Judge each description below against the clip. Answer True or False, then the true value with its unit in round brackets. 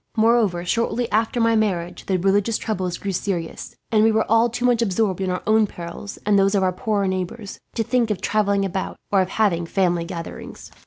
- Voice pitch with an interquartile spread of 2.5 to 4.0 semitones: True (3.2 semitones)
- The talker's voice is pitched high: True (200 Hz)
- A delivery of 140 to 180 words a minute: False (205 wpm)